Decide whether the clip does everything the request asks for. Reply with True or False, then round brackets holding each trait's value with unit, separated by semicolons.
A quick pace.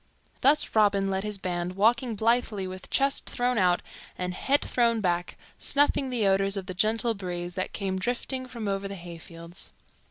False (170 wpm)